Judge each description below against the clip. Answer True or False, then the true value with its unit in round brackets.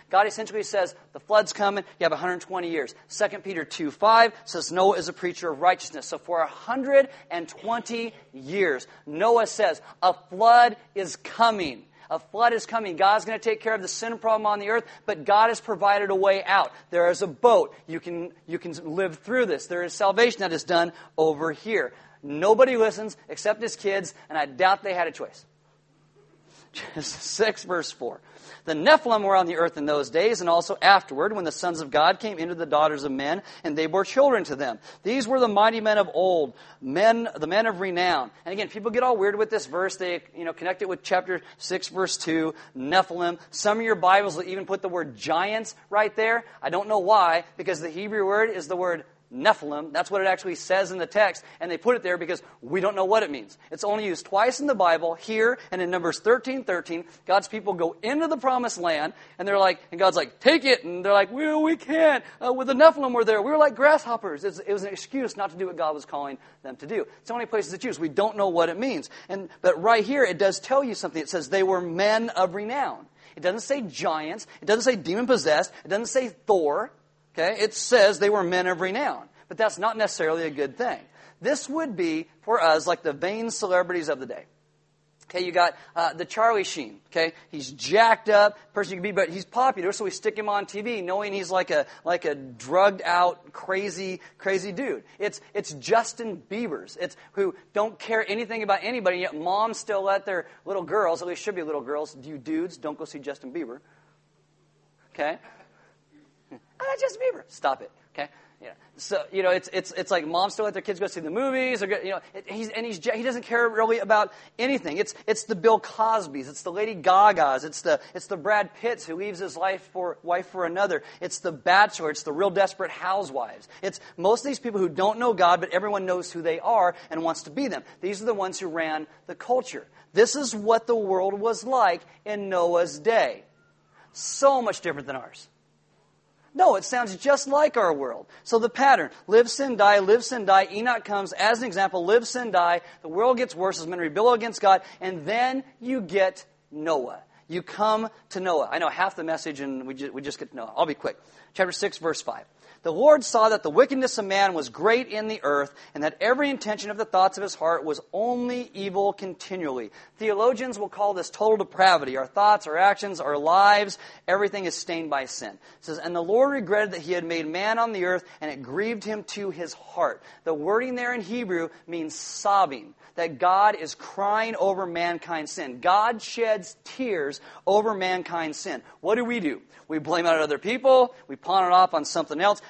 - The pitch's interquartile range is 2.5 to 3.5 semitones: False (4.4 semitones)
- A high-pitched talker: True (195 Hz)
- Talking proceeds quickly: True (215 wpm)